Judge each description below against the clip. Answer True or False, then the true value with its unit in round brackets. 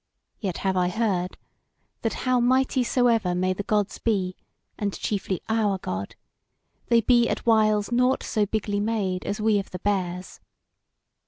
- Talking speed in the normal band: True (155 wpm)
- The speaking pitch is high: True (205 Hz)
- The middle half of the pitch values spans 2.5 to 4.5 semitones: True (3.6 semitones)